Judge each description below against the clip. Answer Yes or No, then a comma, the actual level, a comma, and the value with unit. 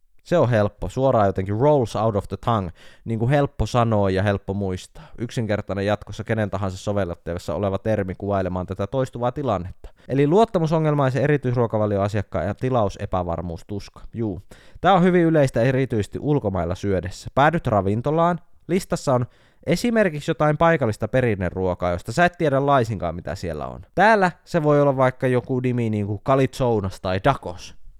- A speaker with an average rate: Yes, average, 145 wpm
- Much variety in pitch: Yes, wide, 5.9 semitones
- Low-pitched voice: Yes, low, 110 Hz